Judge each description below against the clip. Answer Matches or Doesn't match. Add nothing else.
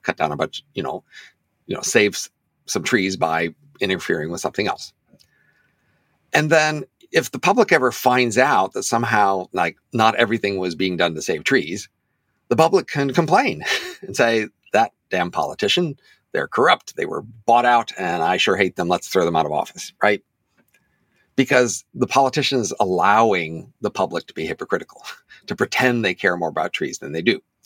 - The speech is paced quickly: Doesn't match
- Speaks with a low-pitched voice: Matches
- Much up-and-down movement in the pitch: Matches